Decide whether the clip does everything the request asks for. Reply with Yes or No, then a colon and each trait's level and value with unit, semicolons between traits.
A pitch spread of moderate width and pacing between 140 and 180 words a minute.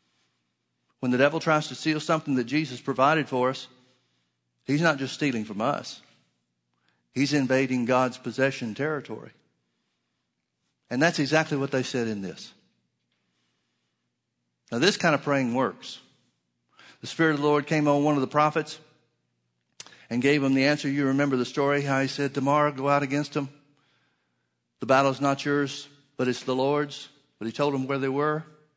No: wide, 7.6 semitones; average, 170 wpm